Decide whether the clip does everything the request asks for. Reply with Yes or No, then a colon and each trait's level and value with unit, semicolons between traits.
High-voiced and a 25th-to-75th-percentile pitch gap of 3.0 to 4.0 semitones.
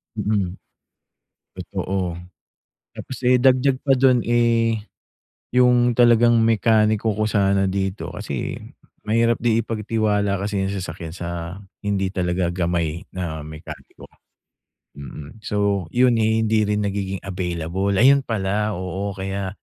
No: low, 100 Hz; average, 3.4 semitones